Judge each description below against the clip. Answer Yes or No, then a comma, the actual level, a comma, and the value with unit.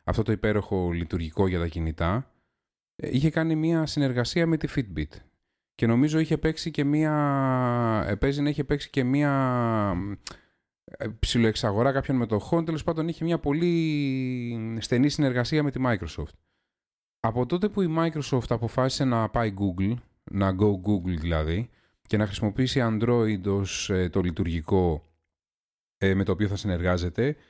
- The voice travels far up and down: Yes, wide, 6.5 semitones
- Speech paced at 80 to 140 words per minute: Yes, average, 135 wpm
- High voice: No, low, 115 Hz